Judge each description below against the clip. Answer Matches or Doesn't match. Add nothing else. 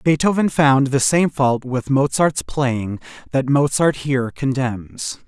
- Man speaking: Matches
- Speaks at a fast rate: Doesn't match